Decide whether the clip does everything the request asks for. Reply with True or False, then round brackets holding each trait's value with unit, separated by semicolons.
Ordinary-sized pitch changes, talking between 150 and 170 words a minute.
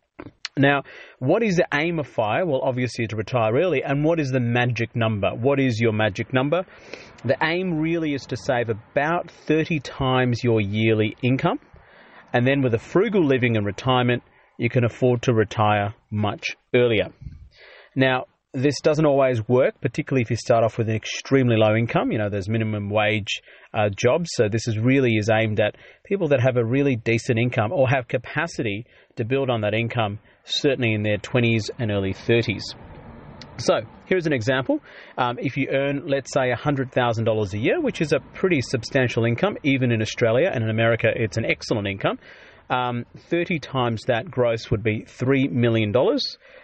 False (3.6 semitones; 180 wpm)